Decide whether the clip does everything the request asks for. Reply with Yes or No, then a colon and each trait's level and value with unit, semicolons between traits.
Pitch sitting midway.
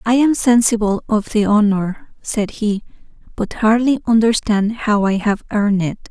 No: high, 215 Hz